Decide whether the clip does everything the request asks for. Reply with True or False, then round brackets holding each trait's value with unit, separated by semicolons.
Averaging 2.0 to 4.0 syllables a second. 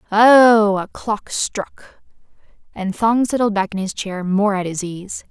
True (3.7 syllables/s)